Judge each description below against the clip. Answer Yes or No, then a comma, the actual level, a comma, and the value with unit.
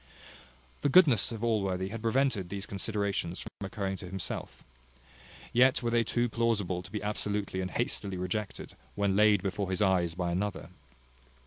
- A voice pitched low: Yes, low, 100 Hz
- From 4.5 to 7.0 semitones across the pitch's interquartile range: No, average, 3.2 semitones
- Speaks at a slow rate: No, average, 155 wpm